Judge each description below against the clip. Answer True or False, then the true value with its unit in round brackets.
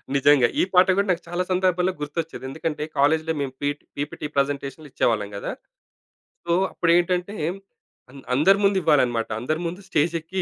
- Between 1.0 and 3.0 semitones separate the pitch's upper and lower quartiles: False (4.2 semitones)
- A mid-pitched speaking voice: True (160 Hz)